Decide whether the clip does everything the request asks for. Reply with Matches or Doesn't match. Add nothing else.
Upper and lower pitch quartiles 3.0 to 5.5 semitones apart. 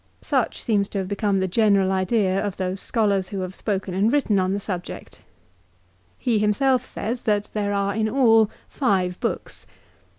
Doesn't match